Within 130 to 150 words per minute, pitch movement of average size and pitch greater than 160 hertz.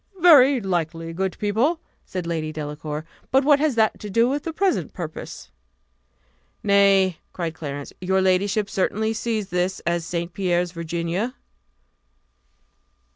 Yes: slow, 135 wpm; average, 4.9 semitones; high, 190 Hz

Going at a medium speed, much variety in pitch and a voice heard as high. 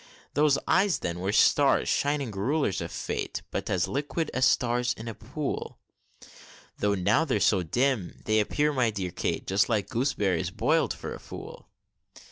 No: average, 165 wpm; wide, 5.9 semitones; low, 115 Hz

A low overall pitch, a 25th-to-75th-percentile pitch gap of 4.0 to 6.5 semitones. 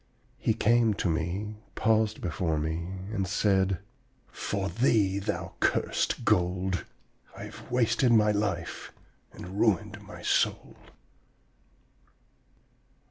No: low, 100 Hz; average, 3.1 semitones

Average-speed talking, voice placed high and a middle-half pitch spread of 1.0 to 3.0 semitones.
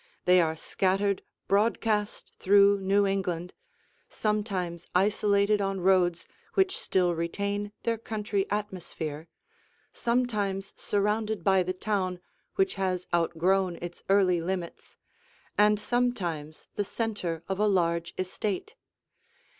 No: slow, 110 wpm; high, 195 Hz; average, 2.7 semitones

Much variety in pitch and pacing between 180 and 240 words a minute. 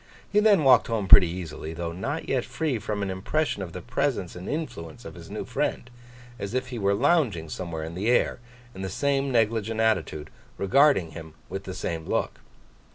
Yes: wide, 6.3 semitones; average, 190 wpm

